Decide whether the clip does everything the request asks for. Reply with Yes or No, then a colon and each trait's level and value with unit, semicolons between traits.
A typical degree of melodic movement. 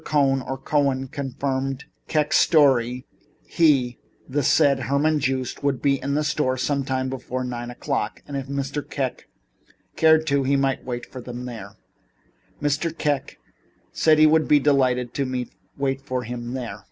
No: narrow, 2.1 semitones